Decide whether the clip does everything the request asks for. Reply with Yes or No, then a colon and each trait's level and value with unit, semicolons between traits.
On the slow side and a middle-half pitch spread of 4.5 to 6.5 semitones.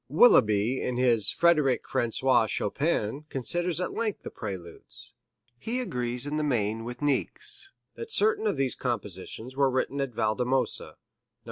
No: average, 145 wpm; average, 5.2 semitones